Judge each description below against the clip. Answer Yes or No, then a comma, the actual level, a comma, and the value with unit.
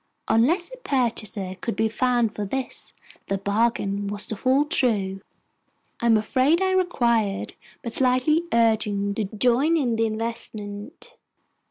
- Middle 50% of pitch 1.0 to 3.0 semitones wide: No, average, 3.8 semitones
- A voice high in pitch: Yes, high, 230 Hz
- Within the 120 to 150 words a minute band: Yes, average, 140 wpm